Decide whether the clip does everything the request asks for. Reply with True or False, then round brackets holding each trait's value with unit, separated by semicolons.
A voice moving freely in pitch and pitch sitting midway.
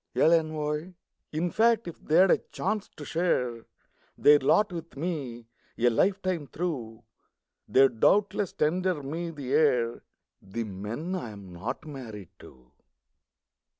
True (6.9 semitones; 150 Hz)